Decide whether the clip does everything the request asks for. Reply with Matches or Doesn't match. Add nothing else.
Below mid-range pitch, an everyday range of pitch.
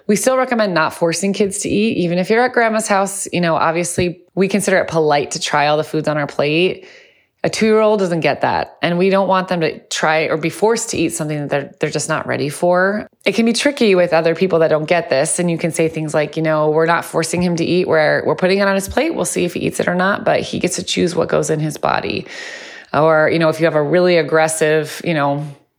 Doesn't match